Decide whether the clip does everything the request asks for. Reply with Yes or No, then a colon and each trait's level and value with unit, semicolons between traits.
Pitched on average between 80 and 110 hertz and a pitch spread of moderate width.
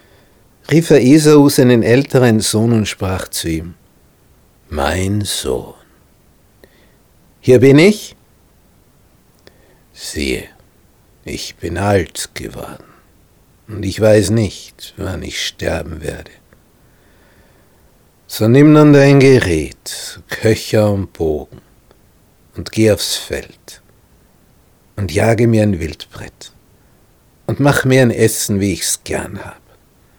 Yes: low, 105 Hz; average, 4.7 semitones